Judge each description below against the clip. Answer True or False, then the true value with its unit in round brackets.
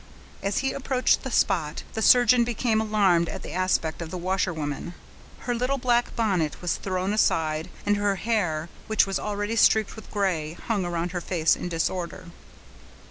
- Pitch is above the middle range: True (195 Hz)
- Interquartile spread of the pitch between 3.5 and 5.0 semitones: True (4.4 semitones)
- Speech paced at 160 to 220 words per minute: True (170 wpm)